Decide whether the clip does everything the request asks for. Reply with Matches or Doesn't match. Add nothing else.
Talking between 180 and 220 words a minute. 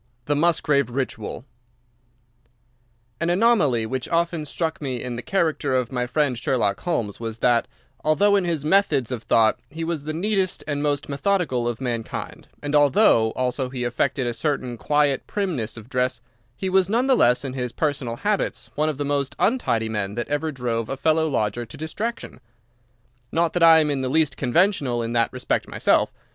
Matches